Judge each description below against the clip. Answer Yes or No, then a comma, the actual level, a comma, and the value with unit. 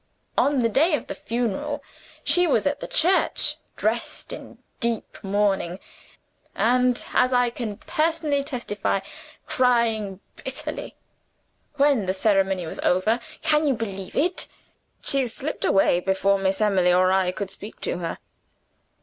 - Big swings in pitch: Yes, wide, 6.3 semitones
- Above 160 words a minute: No, average, 140 wpm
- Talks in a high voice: Yes, high, 225 Hz